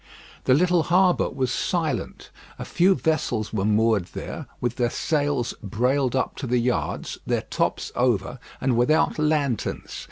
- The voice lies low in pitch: Yes, low, 130 Hz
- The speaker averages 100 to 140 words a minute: No, average, 150 wpm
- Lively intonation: No, average, 4.5 semitones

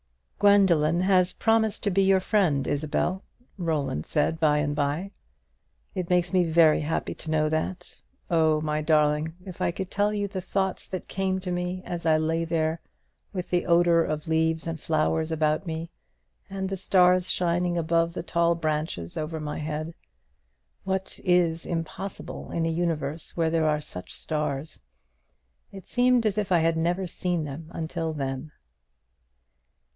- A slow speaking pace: No, average, 160 wpm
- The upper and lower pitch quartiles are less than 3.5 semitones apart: Yes, average, 2.8 semitones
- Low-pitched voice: No, medium, 165 Hz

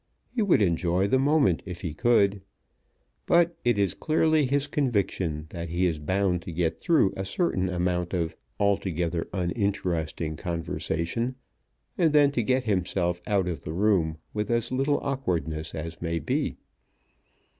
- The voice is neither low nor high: No, very low, 95 Hz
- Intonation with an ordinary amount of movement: No, wide, 6.5 semitones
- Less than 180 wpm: Yes, average, 150 wpm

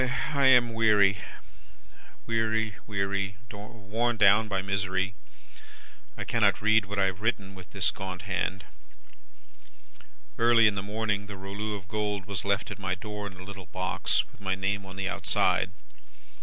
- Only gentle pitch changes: Yes, narrow, 1.9 semitones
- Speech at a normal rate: Yes, average, 155 wpm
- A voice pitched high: No, low, 100 Hz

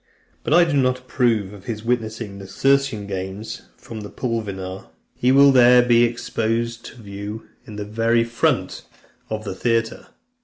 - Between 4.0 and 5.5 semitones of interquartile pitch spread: No, average, 2.9 semitones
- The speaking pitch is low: Yes, low, 115 Hz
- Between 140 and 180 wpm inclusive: Yes, average, 160 wpm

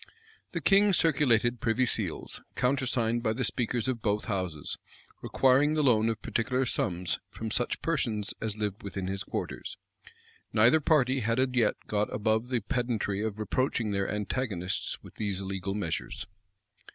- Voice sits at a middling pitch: No, low, 115 Hz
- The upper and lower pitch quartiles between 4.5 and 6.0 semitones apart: No, average, 3.8 semitones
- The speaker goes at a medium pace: Yes, average, 150 wpm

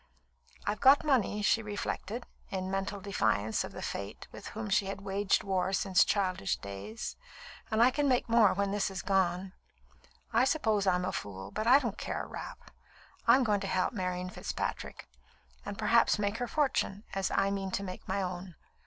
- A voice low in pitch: No, high, 200 Hz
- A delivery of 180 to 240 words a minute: Yes, average, 185 wpm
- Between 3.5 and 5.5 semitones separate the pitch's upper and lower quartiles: No, average, 2.9 semitones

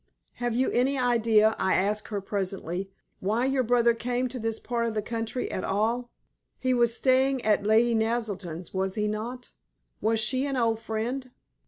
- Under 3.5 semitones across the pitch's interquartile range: Yes, narrow, 2.6 semitones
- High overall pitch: Yes, high, 230 Hz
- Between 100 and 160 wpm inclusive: No, average, 175 wpm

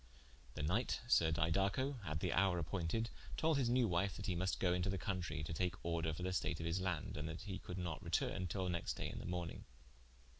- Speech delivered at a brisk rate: Yes, fast, 235 wpm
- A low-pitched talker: Yes, very low, 90 Hz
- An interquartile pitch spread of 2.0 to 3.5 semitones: Yes, average, 2.8 semitones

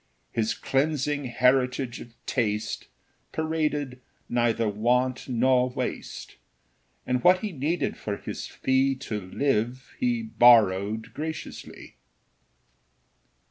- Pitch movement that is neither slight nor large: Yes, average, 3.8 semitones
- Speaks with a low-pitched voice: Yes, low, 125 Hz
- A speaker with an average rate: No, slow, 100 wpm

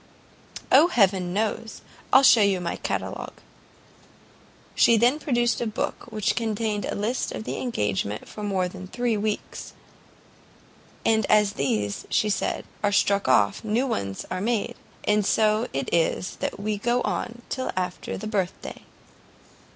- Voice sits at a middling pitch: No, high, 210 Hz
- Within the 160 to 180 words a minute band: No, average, 145 wpm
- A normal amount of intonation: Yes, average, 3.7 semitones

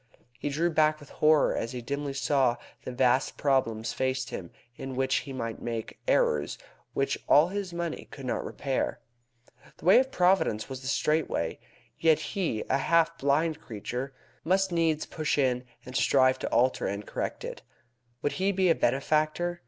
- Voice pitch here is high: No, medium, 140 Hz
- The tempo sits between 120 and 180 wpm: Yes, average, 175 wpm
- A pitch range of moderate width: Yes, average, 4.1 semitones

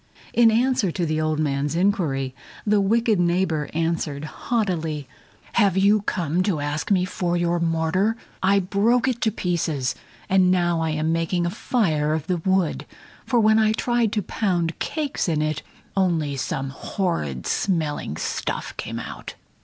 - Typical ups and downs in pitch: Yes, average, 4.4 semitones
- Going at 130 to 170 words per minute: Yes, average, 160 wpm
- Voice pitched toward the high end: No, medium, 175 Hz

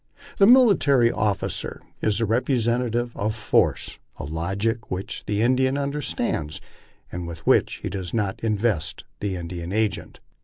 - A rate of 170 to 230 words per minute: No, average, 140 wpm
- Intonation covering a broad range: No, average, 4.4 semitones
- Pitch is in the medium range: No, low, 110 Hz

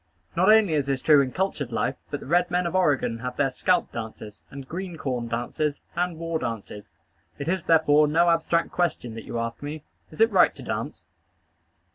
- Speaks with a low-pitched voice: No, medium, 150 Hz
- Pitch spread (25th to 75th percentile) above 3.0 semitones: Yes, wide, 5.4 semitones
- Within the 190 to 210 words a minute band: Yes, average, 200 wpm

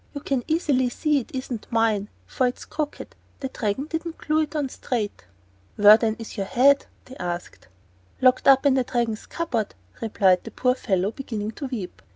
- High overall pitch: Yes, very high, 250 Hz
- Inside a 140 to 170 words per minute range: No, average, 190 wpm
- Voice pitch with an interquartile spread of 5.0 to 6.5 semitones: No, average, 4.4 semitones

